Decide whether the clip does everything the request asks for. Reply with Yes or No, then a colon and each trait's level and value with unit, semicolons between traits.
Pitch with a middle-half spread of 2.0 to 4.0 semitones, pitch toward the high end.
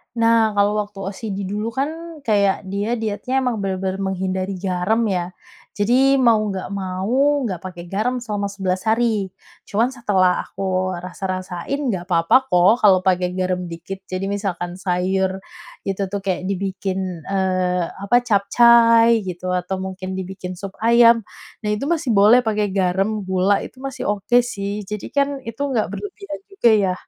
Yes: average, 3.6 semitones; high, 200 Hz